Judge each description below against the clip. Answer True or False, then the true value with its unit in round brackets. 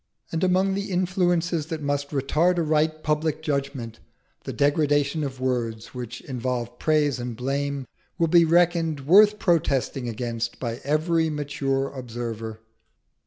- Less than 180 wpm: True (135 wpm)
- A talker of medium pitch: True (145 Hz)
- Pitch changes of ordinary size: True (4.3 semitones)